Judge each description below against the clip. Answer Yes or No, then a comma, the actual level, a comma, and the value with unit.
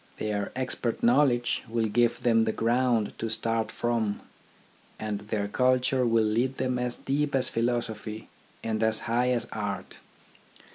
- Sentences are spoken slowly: No, average, 150 wpm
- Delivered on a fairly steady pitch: Yes, narrow, 2.3 semitones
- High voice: No, low, 115 Hz